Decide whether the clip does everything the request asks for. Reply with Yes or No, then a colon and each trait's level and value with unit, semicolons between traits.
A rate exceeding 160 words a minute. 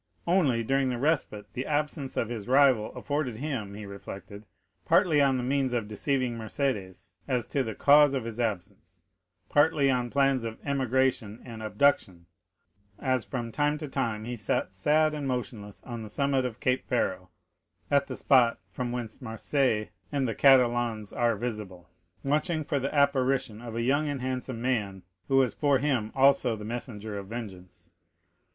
Yes: average, 170 wpm